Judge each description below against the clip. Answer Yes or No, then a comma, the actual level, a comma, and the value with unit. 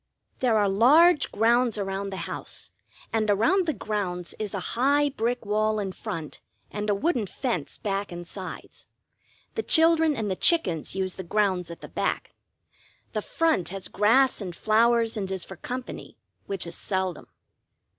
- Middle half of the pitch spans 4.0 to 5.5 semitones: Yes, average, 4.5 semitones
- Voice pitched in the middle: No, high, 210 Hz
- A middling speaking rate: Yes, average, 165 wpm